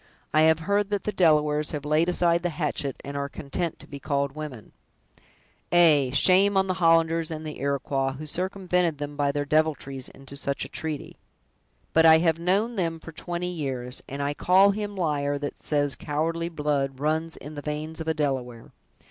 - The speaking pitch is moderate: Yes, medium, 155 Hz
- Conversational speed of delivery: Yes, average, 185 wpm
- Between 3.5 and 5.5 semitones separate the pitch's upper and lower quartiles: No, average, 3.1 semitones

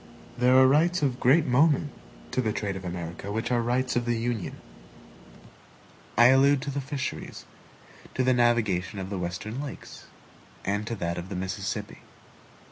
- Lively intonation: No, average, 5.0 semitones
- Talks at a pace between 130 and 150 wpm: No, average, 165 wpm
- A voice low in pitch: Yes, low, 120 Hz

